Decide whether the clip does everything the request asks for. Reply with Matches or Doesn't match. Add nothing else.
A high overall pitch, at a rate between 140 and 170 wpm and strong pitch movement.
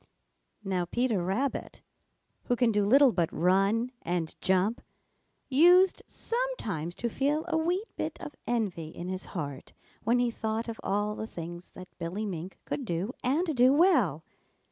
Matches